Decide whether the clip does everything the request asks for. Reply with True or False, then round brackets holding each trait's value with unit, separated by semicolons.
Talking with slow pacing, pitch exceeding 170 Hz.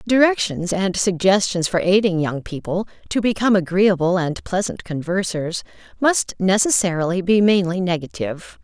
True (125 wpm; 185 Hz)